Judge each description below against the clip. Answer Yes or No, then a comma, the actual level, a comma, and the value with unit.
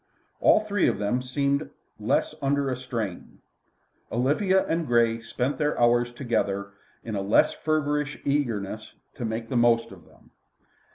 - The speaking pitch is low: Yes, low, 125 Hz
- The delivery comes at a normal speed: Yes, average, 150 wpm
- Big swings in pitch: No, average, 4.1 semitones